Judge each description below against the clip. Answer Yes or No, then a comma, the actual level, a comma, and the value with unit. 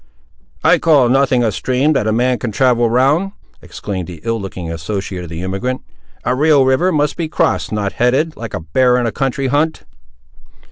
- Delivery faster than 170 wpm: Yes, average, 190 wpm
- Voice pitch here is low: Yes, low, 125 Hz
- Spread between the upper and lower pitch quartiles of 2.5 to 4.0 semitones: No, average, 4.9 semitones